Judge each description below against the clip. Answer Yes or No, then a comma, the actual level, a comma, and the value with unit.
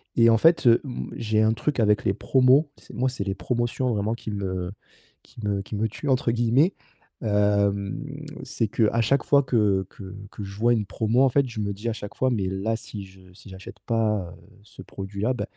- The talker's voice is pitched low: Yes, low, 110 Hz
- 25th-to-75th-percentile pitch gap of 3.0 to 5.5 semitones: Yes, average, 3.3 semitones